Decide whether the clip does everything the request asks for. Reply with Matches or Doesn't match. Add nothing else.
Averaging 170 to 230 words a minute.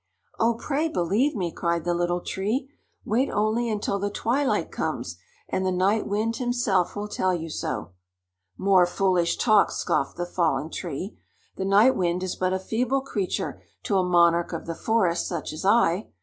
Matches